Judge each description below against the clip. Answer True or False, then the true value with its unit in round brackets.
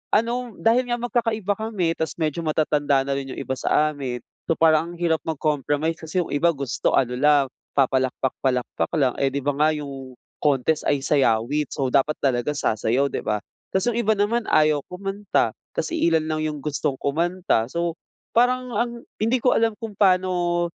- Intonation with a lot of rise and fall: True (5.8 semitones)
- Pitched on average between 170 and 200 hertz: False (155 Hz)